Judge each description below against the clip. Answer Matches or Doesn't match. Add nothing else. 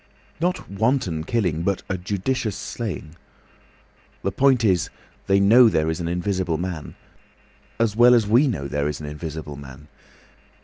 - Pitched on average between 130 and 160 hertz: Doesn't match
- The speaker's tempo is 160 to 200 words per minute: Doesn't match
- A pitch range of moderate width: Doesn't match